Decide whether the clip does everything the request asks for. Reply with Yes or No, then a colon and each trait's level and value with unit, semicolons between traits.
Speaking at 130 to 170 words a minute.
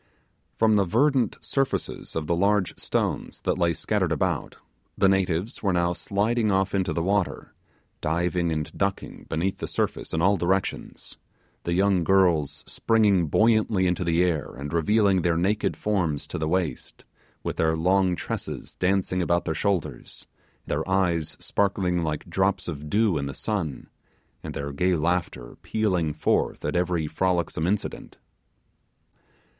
Yes: average, 150 wpm